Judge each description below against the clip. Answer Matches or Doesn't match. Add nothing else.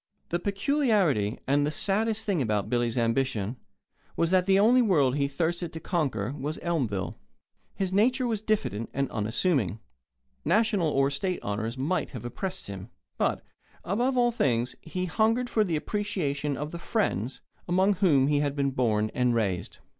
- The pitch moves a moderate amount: Doesn't match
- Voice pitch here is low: Doesn't match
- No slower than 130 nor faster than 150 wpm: Doesn't match